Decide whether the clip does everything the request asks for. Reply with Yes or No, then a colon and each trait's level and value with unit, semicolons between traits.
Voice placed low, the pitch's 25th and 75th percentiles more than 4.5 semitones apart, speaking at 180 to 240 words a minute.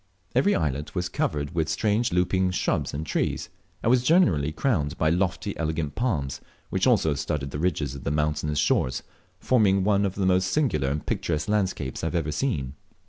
Yes: very low, 80 Hz; average, 5.0 semitones; average, 190 wpm